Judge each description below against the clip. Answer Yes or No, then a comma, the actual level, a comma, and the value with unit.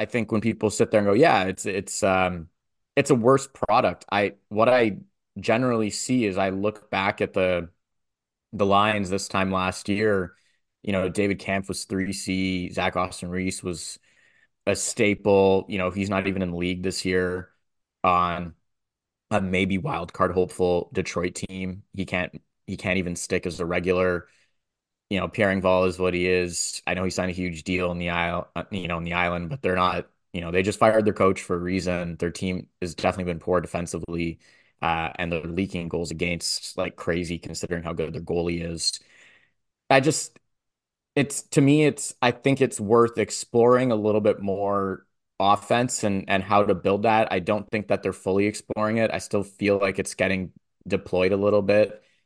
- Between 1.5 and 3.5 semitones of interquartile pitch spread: Yes, narrow, 2.6 semitones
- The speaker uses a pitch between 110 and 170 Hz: No, very low, 95 Hz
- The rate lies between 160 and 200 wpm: Yes, average, 195 wpm